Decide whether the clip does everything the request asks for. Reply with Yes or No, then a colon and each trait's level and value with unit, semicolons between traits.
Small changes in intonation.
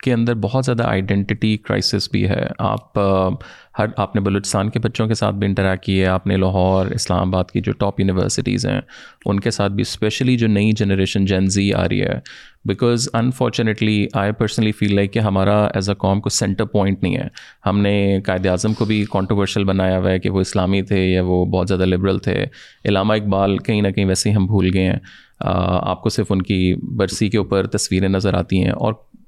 Yes: narrow, 2.2 semitones